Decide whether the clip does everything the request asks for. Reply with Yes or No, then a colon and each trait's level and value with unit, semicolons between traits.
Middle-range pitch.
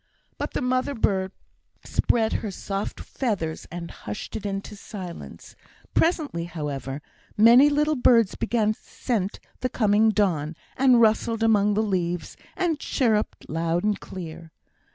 No: high, 210 Hz